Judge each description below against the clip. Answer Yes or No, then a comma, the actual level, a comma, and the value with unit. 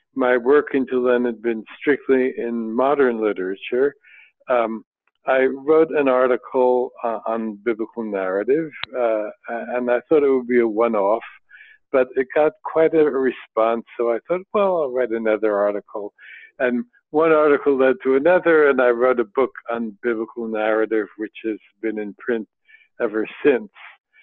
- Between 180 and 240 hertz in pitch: No, low, 125 Hz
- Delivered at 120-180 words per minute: Yes, average, 160 wpm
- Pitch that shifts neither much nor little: Yes, average, 3.9 semitones